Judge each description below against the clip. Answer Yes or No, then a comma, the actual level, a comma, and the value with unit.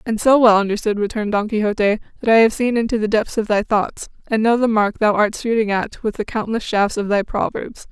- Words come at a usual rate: No, fast, 245 wpm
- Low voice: No, high, 215 Hz